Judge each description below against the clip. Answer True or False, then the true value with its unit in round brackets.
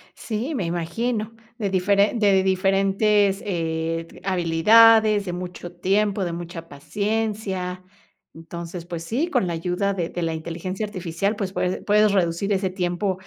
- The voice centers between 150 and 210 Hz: True (190 Hz)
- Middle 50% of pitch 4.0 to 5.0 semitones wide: False (3.2 semitones)